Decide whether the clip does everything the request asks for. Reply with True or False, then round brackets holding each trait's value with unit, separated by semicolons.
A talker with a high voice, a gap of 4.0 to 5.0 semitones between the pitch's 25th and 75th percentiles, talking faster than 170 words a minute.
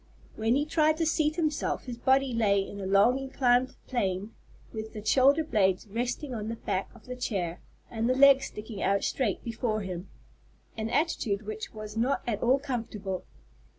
True (230 Hz; 4.3 semitones; 180 wpm)